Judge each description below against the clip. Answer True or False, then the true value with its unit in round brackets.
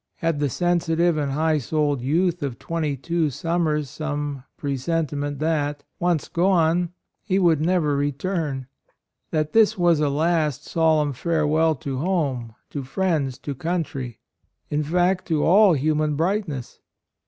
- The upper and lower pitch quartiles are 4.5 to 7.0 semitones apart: False (2.9 semitones)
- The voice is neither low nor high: True (155 Hz)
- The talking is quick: False (140 wpm)